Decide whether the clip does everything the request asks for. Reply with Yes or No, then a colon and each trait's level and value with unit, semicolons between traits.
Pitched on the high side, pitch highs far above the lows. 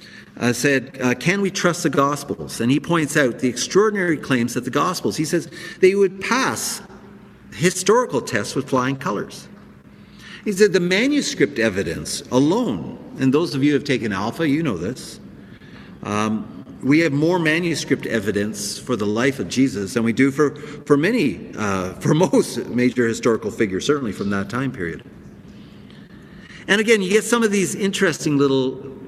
No: medium, 140 Hz; wide, 6.6 semitones